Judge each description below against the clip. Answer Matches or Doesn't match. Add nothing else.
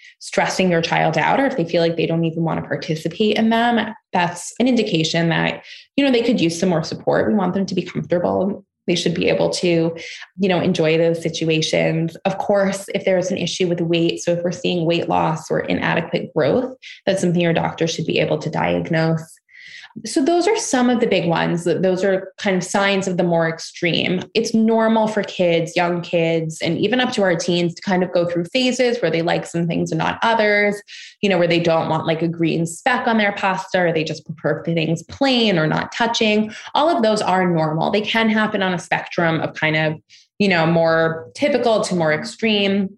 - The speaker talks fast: Matches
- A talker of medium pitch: Matches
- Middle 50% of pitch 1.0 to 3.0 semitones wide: Doesn't match